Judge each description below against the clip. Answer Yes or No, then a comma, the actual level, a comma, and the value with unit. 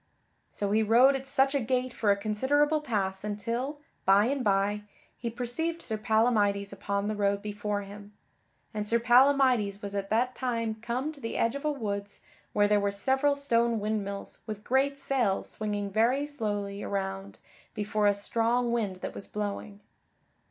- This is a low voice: No, high, 220 Hz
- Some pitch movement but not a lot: Yes, average, 3.8 semitones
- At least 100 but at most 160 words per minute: No, average, 170 wpm